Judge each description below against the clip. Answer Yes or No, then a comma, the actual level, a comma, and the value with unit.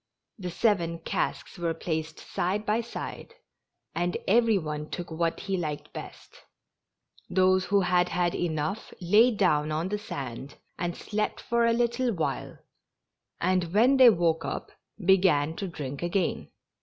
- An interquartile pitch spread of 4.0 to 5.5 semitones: Yes, average, 4.3 semitones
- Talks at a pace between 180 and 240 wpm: No, average, 145 wpm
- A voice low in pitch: No, medium, 180 Hz